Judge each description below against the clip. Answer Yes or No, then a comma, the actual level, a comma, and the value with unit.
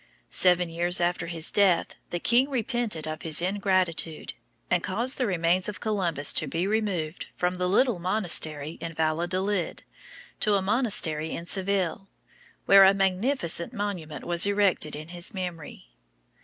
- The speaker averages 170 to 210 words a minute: No, average, 145 wpm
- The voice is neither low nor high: Yes, medium, 180 Hz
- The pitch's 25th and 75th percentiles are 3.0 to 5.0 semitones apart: Yes, average, 3.3 semitones